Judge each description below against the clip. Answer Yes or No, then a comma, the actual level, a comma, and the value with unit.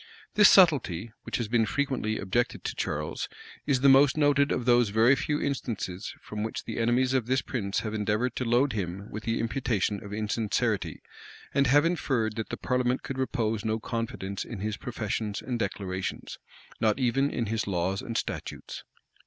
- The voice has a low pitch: Yes, low, 115 Hz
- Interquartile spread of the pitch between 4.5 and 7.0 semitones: No, average, 3.7 semitones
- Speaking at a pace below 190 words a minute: Yes, average, 180 wpm